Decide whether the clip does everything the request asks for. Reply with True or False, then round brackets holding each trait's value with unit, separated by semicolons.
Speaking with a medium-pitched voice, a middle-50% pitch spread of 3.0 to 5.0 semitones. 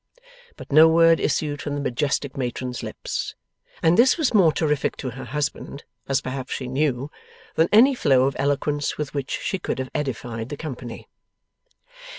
True (145 Hz; 3.3 semitones)